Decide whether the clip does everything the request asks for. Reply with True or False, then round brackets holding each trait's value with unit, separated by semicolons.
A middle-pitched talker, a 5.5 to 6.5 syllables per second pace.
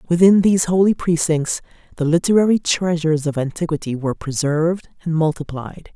True (165 Hz; 5.7 syllables/s)